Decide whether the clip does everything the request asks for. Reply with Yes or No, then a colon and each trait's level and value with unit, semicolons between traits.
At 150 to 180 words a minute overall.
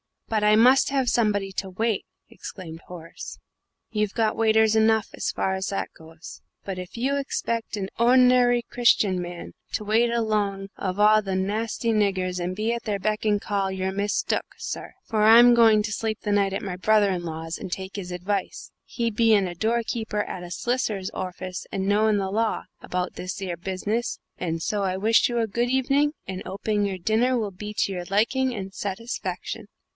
No: average, 190 wpm